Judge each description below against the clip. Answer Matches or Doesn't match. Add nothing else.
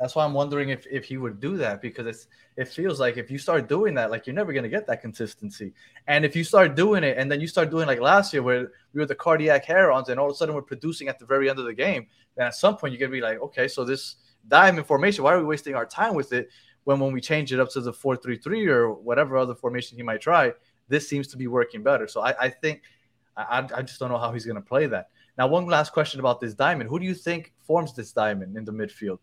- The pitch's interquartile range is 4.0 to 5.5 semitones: Matches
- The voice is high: Doesn't match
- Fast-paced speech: Matches